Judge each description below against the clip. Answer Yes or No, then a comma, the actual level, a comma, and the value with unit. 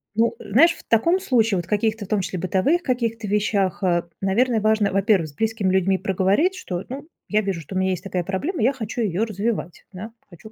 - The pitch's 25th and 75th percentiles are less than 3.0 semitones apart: No, average, 3.4 semitones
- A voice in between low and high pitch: No, high, 210 Hz